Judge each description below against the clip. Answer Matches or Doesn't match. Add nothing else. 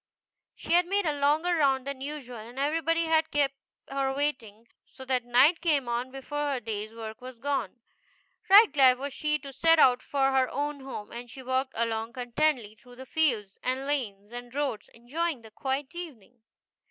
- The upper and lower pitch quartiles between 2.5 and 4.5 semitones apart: Matches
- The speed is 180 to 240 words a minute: Matches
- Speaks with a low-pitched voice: Doesn't match